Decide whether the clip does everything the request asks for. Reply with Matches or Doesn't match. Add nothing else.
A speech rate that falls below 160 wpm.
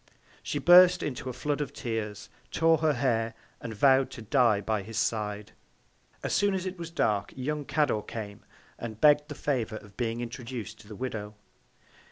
Doesn't match